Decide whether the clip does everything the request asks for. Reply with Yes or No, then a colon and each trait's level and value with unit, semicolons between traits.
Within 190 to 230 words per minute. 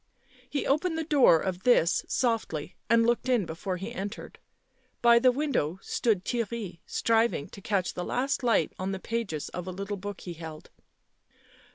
No: average, 170 wpm